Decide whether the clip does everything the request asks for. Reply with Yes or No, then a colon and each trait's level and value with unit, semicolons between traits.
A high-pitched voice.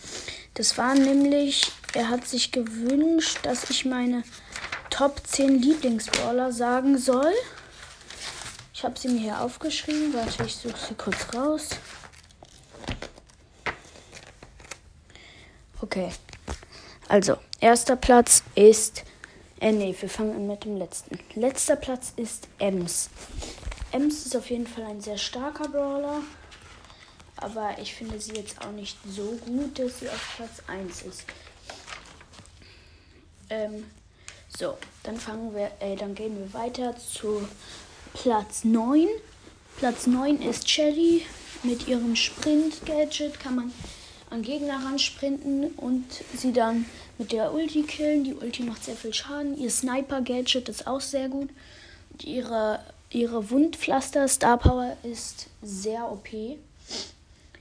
Yes: high, 245 Hz